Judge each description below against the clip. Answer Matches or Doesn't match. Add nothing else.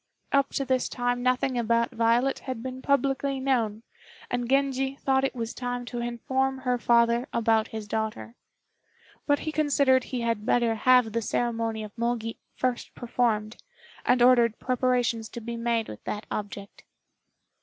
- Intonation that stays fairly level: Matches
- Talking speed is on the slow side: Doesn't match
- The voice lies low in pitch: Doesn't match